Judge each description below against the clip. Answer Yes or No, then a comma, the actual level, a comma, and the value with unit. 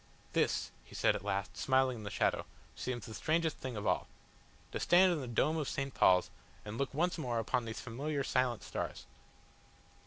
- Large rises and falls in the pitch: No, average, 5.0 semitones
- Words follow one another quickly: No, average, 190 wpm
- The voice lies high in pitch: No, low, 130 Hz